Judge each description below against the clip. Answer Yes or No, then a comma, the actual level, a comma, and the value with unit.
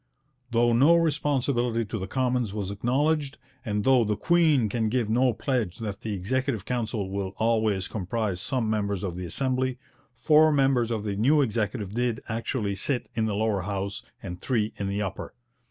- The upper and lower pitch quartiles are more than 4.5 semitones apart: No, average, 4.0 semitones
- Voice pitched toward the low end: Yes, low, 115 Hz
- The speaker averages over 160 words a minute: Yes, average, 175 wpm